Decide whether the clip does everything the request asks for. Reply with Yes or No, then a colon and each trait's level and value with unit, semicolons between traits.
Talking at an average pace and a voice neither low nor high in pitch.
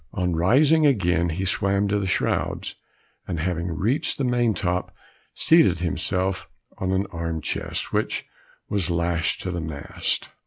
No: average, 150 wpm; very low, 90 Hz